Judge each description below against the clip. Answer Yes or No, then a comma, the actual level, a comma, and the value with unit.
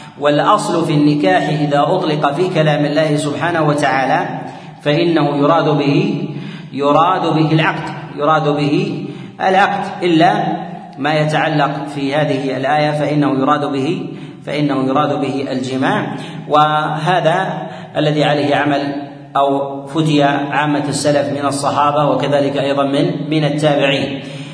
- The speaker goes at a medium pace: Yes, average, 115 wpm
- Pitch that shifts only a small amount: Yes, narrow, 1.7 semitones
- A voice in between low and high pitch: Yes, medium, 150 Hz